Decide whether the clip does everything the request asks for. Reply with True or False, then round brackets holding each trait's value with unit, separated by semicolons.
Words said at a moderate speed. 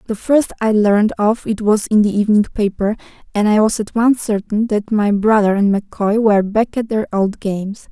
False (210 wpm)